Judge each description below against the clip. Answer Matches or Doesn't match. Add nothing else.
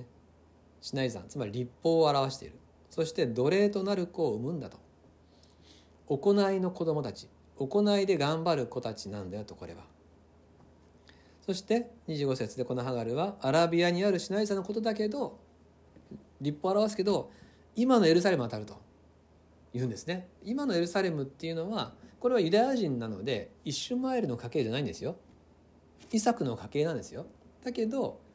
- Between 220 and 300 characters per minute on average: Doesn't match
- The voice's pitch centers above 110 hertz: Matches